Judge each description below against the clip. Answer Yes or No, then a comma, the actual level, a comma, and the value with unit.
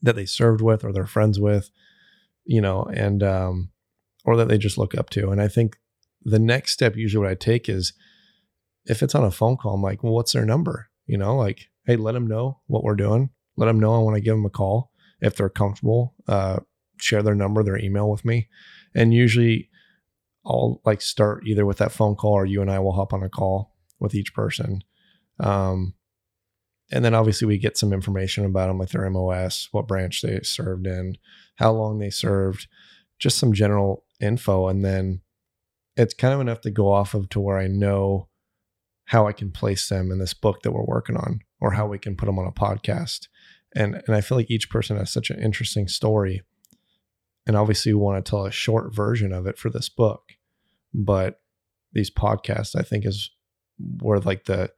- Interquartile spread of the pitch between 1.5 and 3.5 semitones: Yes, narrow, 2.4 semitones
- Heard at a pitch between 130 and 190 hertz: No, low, 105 Hz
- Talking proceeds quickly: Yes, fast, 210 wpm